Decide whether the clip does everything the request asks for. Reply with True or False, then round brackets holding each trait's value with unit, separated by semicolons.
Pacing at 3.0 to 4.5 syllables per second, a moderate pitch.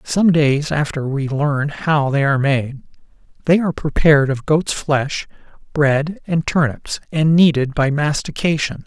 True (4.4 syllables/s; 150 Hz)